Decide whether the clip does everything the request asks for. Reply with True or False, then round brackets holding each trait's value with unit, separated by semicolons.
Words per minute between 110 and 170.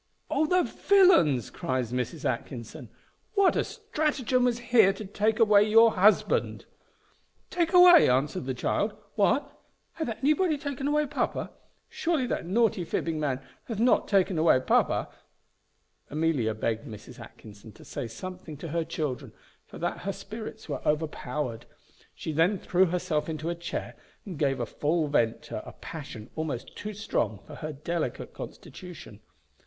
True (150 wpm)